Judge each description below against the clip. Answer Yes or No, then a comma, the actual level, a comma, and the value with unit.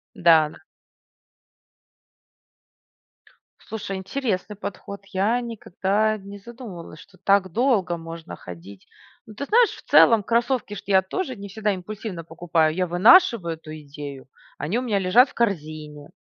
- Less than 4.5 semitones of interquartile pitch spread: No, average, 5.0 semitones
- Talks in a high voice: Yes, high, 195 Hz